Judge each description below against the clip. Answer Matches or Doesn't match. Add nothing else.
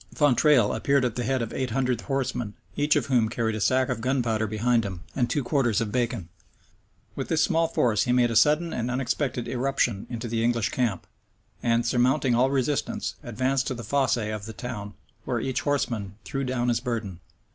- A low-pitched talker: Matches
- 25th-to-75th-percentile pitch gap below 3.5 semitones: Matches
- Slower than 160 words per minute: Doesn't match